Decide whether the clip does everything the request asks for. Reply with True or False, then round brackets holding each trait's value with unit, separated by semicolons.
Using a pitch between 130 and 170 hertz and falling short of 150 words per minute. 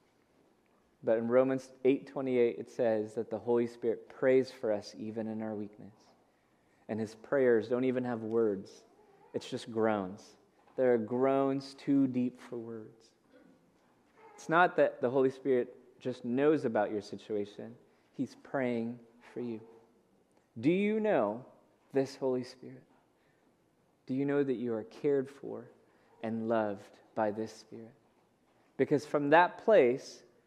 False (120 Hz; 140 wpm)